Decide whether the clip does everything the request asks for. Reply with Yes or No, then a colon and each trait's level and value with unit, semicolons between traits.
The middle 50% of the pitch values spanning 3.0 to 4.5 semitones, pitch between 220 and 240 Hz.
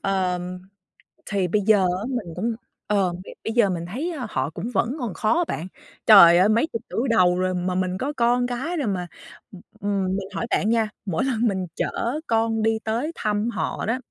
No: average, 4.2 semitones; high, 210 Hz